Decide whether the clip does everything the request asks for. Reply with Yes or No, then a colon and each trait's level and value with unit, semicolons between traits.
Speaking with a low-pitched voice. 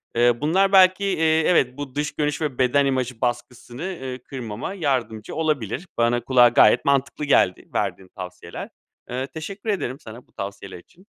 Yes: low, 130 Hz